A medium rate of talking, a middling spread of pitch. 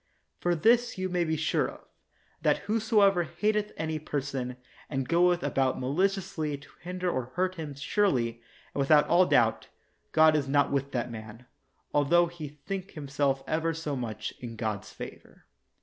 Yes: average, 165 wpm; average, 4.8 semitones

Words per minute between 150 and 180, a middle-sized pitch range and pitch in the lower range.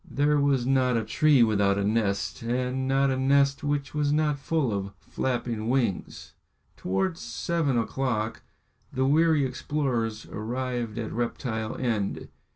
No: average, 140 wpm; average, 3.9 semitones; low, 130 Hz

